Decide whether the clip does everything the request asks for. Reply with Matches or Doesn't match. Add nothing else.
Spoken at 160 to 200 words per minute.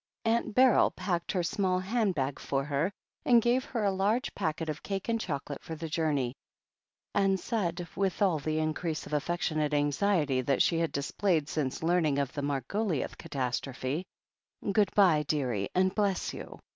Matches